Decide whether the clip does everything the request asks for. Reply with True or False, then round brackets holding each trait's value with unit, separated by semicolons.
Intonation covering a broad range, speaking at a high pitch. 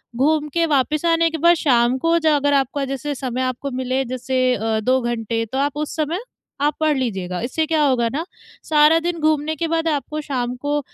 False (3.7 semitones; 285 Hz)